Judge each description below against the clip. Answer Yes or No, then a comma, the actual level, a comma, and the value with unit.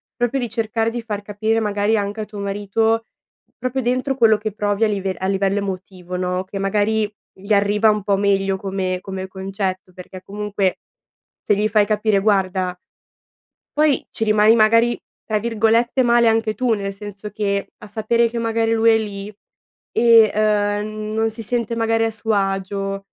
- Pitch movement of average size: No, narrow, 2.3 semitones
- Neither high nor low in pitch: No, high, 210 Hz